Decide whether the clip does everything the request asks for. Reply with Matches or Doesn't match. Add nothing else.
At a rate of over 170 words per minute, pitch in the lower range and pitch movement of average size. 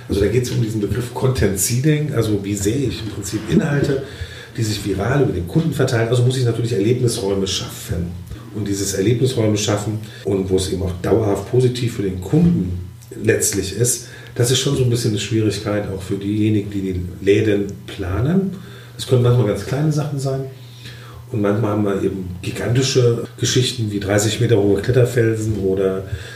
Matches